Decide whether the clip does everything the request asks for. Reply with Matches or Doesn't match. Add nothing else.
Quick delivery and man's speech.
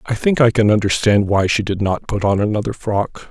Matches